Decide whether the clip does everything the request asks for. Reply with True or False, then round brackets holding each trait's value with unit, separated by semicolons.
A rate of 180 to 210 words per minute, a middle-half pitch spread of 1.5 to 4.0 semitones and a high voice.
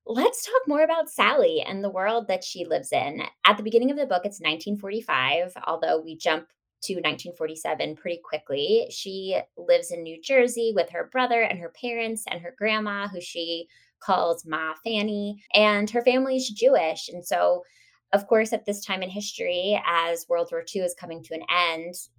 False (185 wpm; 5.5 semitones; 200 Hz)